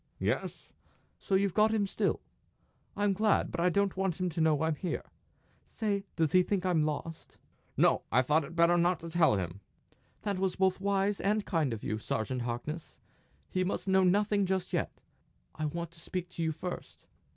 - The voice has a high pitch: No, medium, 180 Hz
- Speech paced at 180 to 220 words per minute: Yes, average, 190 wpm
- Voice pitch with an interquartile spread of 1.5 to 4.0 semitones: Yes, average, 3.5 semitones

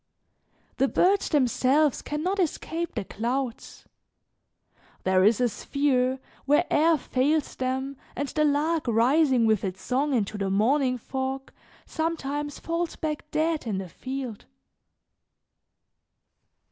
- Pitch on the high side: Yes, very high, 270 Hz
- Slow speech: Yes, slow, 120 wpm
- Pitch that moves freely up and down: No, average, 3.9 semitones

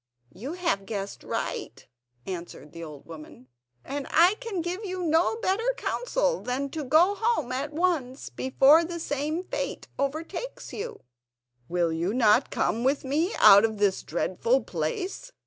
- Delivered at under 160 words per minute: Yes, average, 150 wpm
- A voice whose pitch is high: Yes, very high, 280 Hz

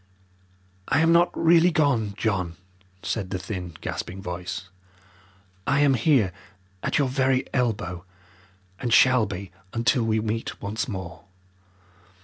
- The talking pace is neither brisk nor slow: No, slow, 130 wpm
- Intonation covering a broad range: Yes, wide, 5.9 semitones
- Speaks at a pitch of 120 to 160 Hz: No, low, 110 Hz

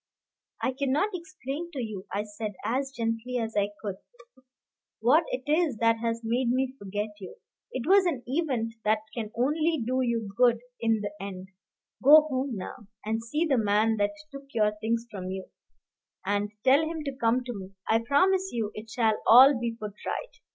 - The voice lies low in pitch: No, high, 235 Hz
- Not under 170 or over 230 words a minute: Yes, average, 185 wpm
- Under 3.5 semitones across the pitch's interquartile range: No, average, 4.2 semitones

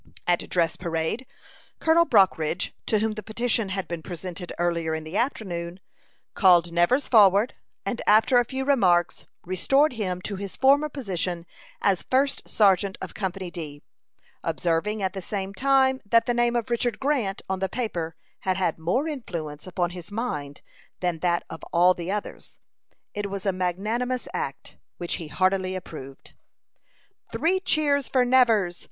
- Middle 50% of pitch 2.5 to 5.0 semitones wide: No, wide, 5.6 semitones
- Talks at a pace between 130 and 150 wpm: No, average, 160 wpm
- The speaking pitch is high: Yes, high, 195 Hz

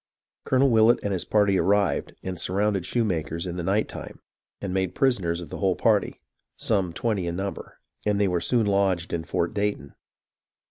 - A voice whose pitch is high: No, very low, 95 Hz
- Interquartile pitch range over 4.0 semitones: No, average, 2.9 semitones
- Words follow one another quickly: No, average, 180 wpm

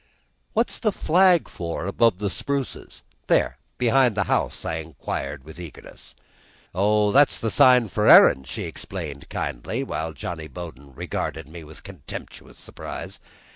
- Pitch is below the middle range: Yes, very low, 90 Hz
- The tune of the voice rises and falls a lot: Yes, wide, 7.9 semitones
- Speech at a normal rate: Yes, average, 145 wpm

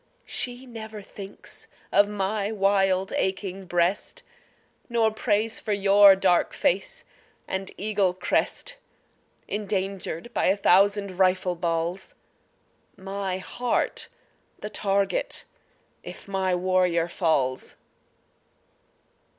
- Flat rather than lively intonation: Yes, narrow, 2.0 semitones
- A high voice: Yes, high, 195 Hz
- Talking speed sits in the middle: No, slow, 95 wpm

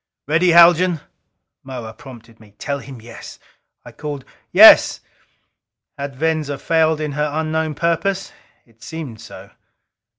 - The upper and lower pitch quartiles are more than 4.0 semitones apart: No, average, 3.7 semitones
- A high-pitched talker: No, medium, 150 Hz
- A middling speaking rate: No, slow, 125 wpm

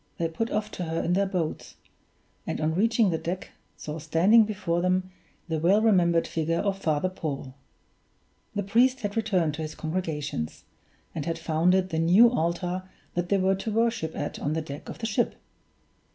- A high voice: No, medium, 175 Hz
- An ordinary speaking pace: Yes, average, 180 wpm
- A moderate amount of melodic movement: Yes, average, 3.9 semitones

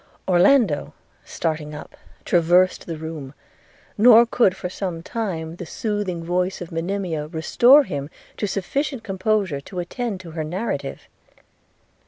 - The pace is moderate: No, slow, 130 wpm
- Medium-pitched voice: Yes, medium, 180 Hz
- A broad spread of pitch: No, average, 4.3 semitones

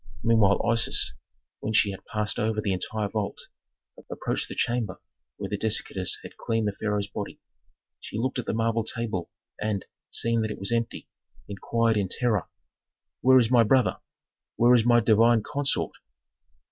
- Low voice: Yes, low, 110 Hz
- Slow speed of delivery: No, average, 160 wpm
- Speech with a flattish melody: Yes, narrow, 2.1 semitones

